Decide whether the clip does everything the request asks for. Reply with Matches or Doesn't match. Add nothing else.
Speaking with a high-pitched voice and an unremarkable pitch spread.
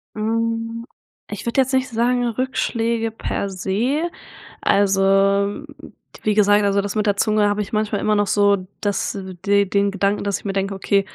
Doesn't match